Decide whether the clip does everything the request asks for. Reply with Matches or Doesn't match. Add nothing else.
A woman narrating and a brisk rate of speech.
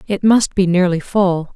Doesn't match